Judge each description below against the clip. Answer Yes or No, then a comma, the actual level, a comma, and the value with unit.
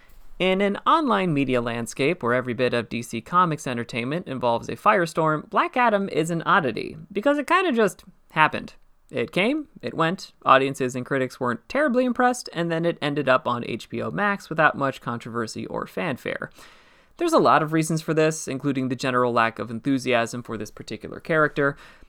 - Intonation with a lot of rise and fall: Yes, wide, 7.0 semitones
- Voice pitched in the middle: Yes, medium, 145 Hz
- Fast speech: No, average, 180 wpm